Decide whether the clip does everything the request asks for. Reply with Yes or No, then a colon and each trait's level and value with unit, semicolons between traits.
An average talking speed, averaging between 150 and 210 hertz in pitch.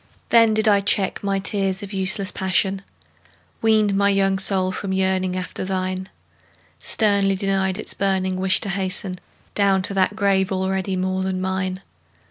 Yes: average, 155 wpm; high, 190 Hz